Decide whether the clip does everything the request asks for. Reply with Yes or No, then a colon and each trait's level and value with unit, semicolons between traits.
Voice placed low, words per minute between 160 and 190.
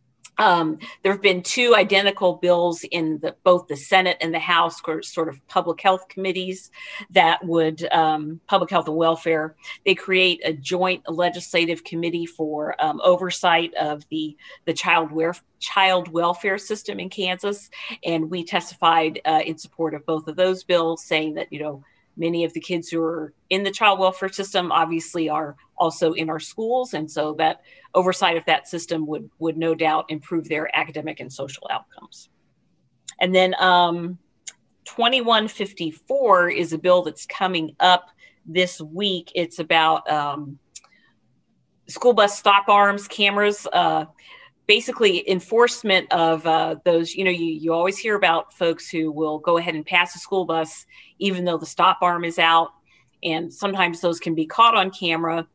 No: medium, 170 Hz; average, 165 wpm